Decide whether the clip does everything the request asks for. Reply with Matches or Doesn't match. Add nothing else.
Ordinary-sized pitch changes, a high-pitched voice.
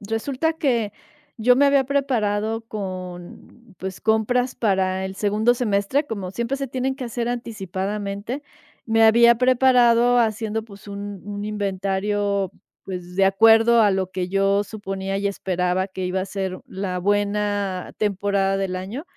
Matches